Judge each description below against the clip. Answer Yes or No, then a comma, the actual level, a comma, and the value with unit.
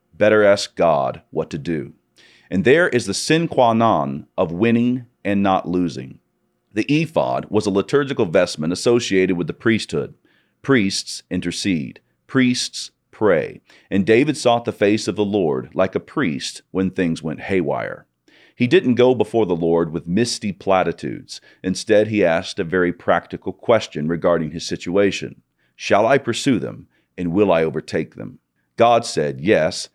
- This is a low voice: Yes, low, 100 Hz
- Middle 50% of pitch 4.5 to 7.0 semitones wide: Yes, average, 4.8 semitones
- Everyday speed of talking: Yes, average, 155 wpm